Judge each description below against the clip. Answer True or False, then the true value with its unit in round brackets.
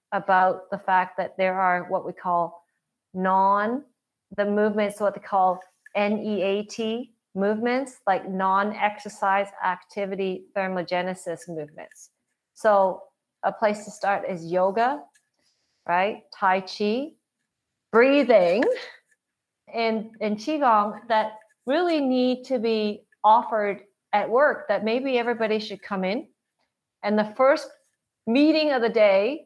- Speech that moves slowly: True (115 wpm)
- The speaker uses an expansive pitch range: False (3.5 semitones)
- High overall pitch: True (210 Hz)